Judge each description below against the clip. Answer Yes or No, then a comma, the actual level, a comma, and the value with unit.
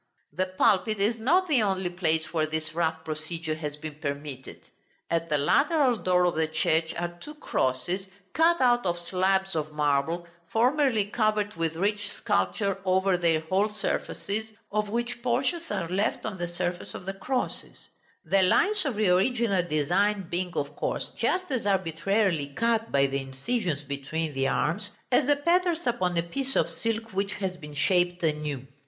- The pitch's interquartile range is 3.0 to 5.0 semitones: No, wide, 5.6 semitones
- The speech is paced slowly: No, average, 170 wpm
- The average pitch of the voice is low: No, medium, 185 Hz